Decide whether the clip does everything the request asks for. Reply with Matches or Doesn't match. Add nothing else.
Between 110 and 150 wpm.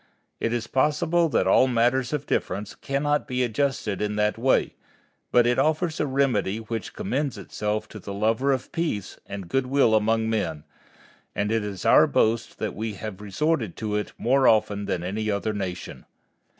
Doesn't match